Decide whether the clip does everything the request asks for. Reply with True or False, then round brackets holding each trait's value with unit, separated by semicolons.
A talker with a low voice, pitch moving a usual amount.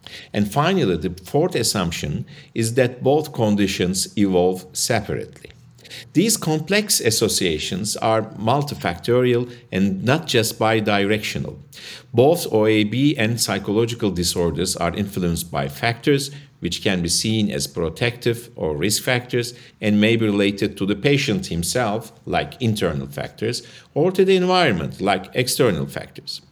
True (110 Hz; 3.9 semitones)